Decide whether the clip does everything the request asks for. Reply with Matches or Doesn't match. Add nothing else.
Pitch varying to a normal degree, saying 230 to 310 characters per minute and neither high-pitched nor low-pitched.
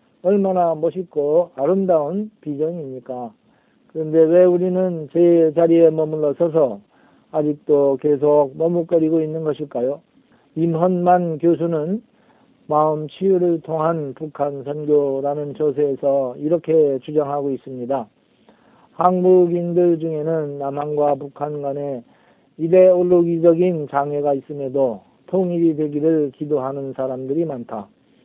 Matches